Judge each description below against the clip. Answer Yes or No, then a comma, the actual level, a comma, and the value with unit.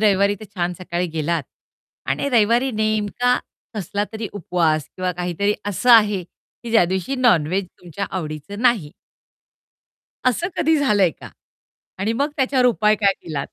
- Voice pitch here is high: Yes, high, 205 Hz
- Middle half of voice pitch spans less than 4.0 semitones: No, average, 4.5 semitones